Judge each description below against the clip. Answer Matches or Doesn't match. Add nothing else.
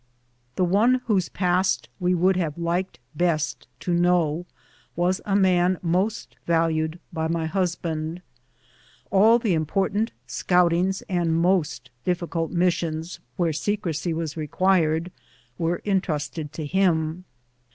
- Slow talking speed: Matches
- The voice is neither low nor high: Matches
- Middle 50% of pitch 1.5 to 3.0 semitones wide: Matches